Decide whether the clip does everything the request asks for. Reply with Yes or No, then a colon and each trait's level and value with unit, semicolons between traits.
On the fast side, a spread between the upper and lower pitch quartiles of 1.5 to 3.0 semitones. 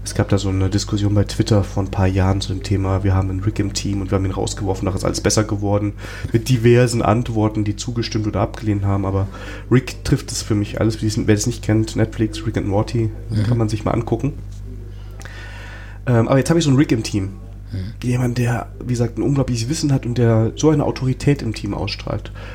Yes: fast, 225 wpm; narrow, 2.6 semitones